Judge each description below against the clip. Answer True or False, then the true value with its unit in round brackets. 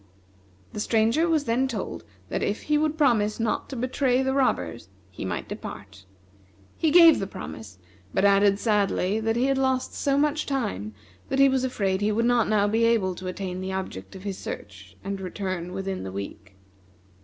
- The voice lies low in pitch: False (210 Hz)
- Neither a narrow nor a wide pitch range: False (5.9 semitones)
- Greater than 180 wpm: True (190 wpm)